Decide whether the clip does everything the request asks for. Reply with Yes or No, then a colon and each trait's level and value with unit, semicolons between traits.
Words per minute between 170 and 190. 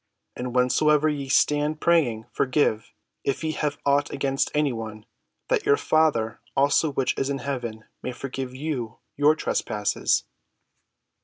No: average, 140 wpm